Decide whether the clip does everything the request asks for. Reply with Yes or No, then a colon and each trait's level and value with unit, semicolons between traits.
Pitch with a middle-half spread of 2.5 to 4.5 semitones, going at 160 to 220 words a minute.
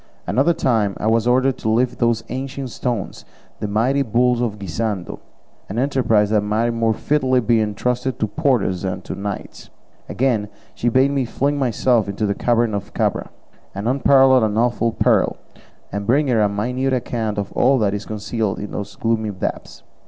Yes: average, 3.6 semitones; average, 175 wpm